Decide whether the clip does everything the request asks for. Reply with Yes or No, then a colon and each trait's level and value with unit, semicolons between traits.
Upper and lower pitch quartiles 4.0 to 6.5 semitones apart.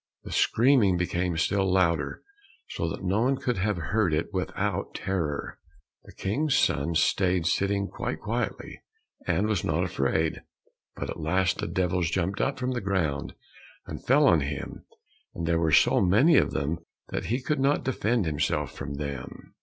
Yes: average, 4.5 semitones